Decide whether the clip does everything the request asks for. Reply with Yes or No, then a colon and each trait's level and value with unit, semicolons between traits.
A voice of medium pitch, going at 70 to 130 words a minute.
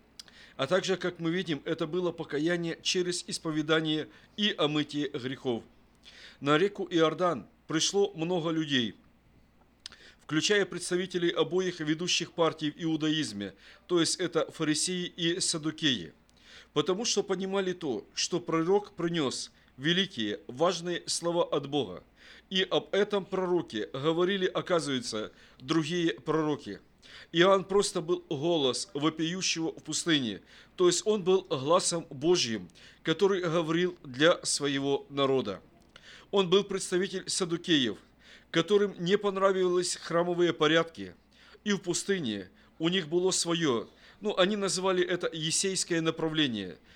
Yes: medium, 170 Hz; average, 120 wpm